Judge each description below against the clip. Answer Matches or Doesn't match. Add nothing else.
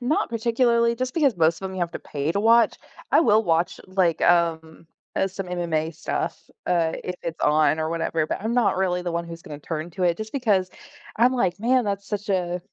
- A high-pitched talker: Doesn't match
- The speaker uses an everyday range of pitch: Matches